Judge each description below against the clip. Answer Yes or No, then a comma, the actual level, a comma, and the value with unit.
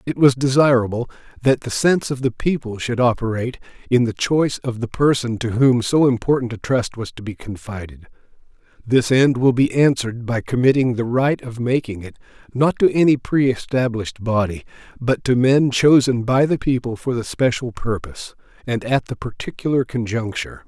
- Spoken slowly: No, average, 175 wpm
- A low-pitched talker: Yes, low, 120 Hz